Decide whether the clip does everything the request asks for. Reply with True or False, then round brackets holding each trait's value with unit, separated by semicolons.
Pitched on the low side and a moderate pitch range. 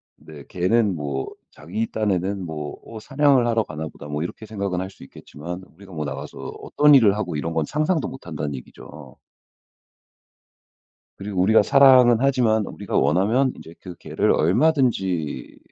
False (95 Hz; 6.9 semitones)